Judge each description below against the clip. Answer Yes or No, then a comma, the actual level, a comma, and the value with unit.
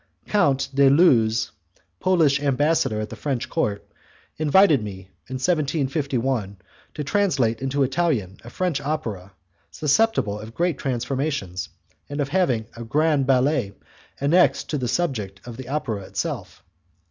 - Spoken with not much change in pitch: No, average, 5.2 semitones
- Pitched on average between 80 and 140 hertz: Yes, low, 135 Hz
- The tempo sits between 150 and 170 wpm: No, slow, 135 wpm